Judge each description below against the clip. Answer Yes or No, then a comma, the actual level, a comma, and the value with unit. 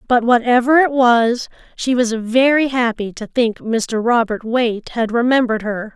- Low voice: No, high, 235 Hz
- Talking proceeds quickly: No, average, 160 wpm